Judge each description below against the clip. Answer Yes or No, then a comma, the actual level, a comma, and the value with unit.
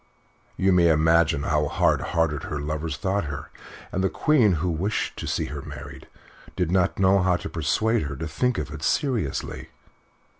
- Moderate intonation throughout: Yes, average, 4.1 semitones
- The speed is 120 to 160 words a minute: No, average, 180 wpm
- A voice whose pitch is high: No, very low, 80 Hz